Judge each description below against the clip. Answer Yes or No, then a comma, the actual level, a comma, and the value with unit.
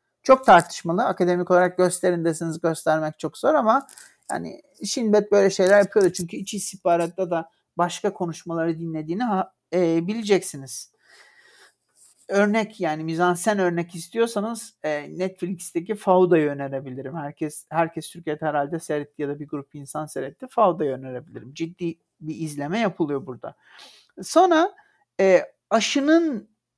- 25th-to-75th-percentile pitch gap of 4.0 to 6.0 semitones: Yes, average, 4.5 semitones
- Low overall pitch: No, medium, 175 Hz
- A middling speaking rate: Yes, average, 115 wpm